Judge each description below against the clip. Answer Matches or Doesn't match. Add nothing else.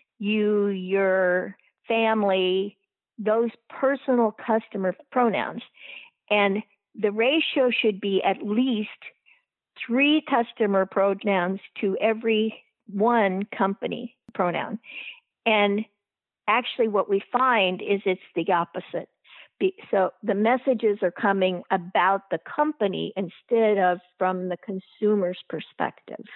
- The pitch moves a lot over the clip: Doesn't match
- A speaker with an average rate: Doesn't match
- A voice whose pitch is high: Matches